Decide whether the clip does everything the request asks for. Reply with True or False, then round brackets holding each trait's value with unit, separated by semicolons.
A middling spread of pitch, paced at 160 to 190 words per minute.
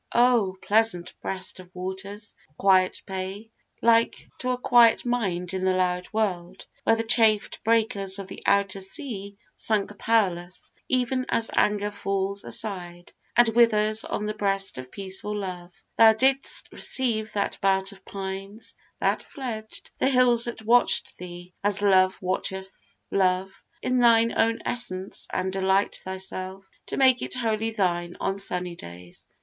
False (3.2 semitones; 145 wpm)